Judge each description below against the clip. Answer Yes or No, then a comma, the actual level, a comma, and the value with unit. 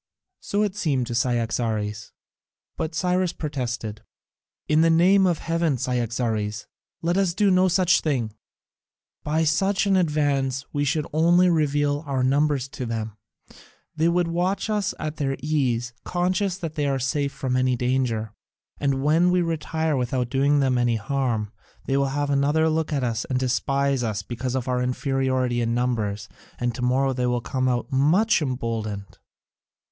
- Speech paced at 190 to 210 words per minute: No, average, 160 wpm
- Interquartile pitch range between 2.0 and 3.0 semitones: No, average, 4.6 semitones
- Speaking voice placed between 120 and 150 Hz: Yes, low, 135 Hz